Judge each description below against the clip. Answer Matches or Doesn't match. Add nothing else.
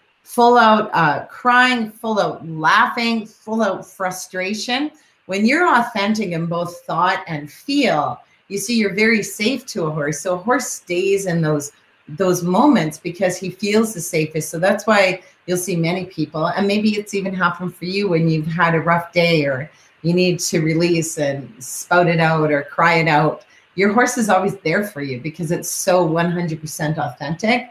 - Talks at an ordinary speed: Matches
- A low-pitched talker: Doesn't match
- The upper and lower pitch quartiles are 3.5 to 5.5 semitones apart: Matches